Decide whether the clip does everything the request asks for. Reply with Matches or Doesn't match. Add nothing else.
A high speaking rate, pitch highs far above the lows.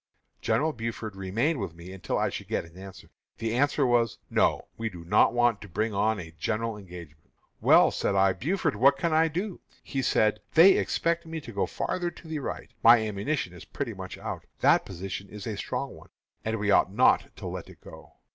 Matches